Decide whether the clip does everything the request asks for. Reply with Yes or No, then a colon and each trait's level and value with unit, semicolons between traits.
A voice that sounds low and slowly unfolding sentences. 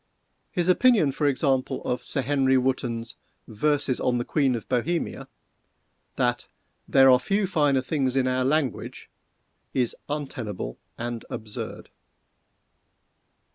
Yes: low, 130 Hz; slow, 115 wpm